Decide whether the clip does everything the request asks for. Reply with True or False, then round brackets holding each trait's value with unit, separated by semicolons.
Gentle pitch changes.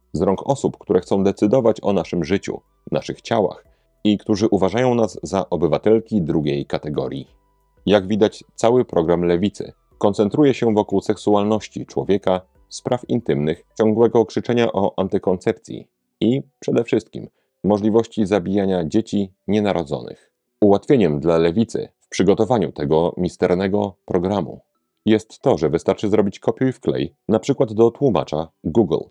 False (3.6 semitones)